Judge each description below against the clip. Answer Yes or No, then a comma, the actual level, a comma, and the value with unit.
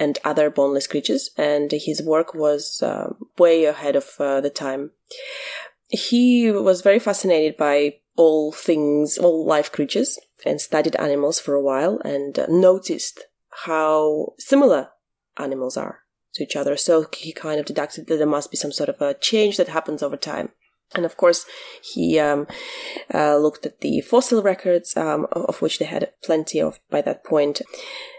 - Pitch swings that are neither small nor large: No, wide, 7.1 semitones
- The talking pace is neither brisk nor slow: Yes, average, 170 wpm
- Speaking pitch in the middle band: Yes, medium, 155 Hz